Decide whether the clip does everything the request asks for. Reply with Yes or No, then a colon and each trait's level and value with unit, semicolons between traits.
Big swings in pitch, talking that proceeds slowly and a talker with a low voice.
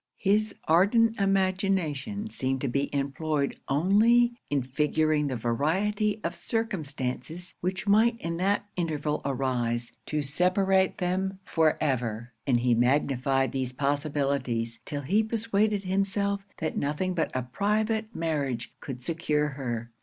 No: wide, 6.6 semitones; slow, 130 wpm; medium, 155 Hz